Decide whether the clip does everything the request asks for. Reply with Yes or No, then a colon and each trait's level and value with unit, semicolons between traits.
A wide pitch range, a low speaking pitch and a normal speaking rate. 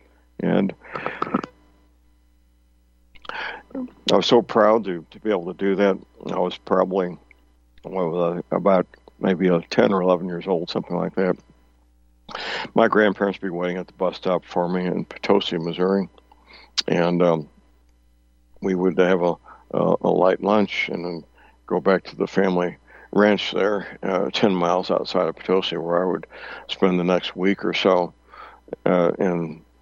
Yes: wide, 7.8 semitones; very low, 90 Hz; average, 155 wpm